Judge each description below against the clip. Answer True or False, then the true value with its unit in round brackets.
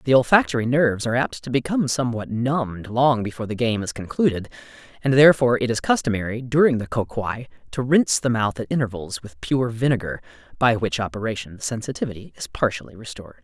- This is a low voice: True (120 Hz)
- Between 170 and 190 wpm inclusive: True (185 wpm)